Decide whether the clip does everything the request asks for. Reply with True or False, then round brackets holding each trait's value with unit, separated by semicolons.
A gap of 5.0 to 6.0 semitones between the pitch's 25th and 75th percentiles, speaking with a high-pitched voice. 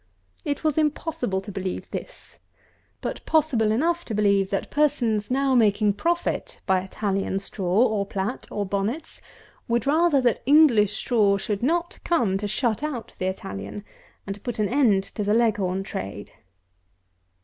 True (5.6 semitones; 215 Hz)